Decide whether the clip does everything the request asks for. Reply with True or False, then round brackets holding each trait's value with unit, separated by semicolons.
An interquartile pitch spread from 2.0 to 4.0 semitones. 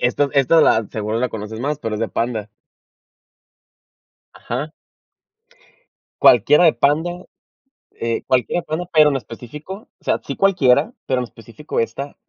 False (4.9 semitones)